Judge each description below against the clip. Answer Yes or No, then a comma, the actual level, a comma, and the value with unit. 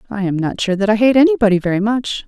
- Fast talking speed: Yes, fast, 265 wpm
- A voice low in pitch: No, high, 215 Hz